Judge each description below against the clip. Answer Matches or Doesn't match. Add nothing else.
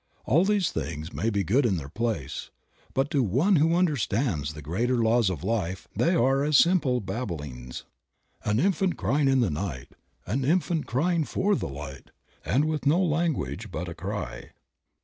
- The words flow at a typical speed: Matches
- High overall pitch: Doesn't match